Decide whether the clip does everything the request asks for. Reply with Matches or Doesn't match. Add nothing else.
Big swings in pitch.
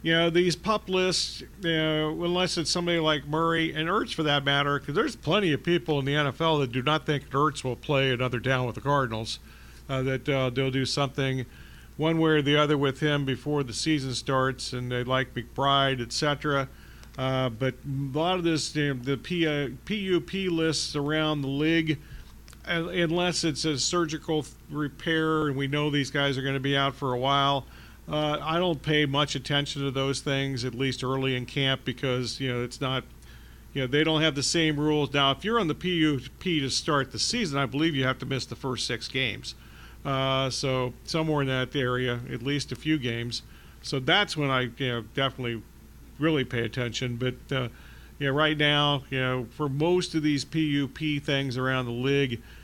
Doesn't match